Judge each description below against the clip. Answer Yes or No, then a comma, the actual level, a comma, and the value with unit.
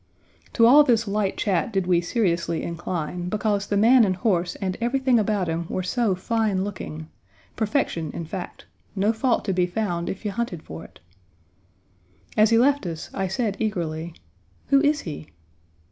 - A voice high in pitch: Yes, high, 195 Hz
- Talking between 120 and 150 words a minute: No, average, 170 wpm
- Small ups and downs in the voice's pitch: No, average, 4.5 semitones